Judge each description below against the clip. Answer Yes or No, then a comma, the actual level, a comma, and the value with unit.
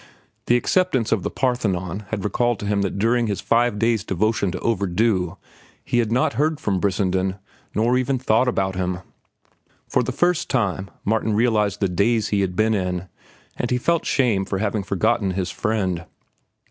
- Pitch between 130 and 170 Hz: No, low, 105 Hz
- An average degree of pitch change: Yes, average, 3.9 semitones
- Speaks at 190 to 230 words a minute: No, average, 175 wpm